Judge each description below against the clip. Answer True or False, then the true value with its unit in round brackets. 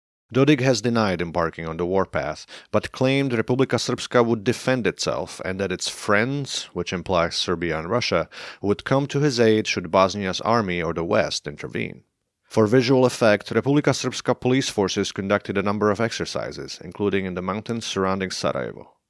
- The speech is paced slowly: False (165 wpm)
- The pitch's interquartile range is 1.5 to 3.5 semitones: False (5.1 semitones)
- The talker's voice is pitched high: False (105 Hz)